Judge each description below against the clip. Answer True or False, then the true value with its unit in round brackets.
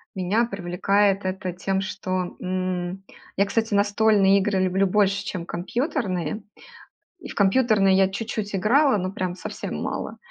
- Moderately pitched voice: False (195 Hz)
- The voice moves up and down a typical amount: False (2.1 semitones)